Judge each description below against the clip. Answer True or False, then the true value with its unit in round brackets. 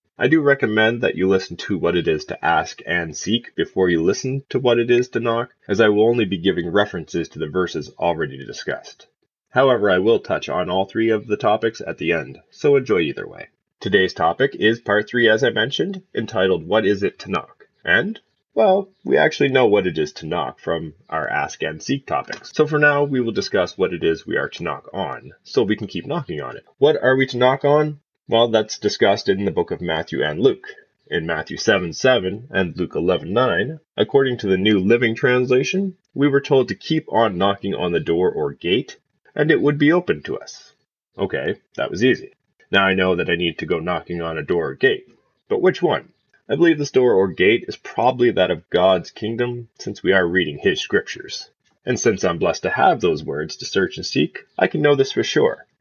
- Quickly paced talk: True (225 wpm)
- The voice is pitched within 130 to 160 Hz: False (120 Hz)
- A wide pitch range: True (6.6 semitones)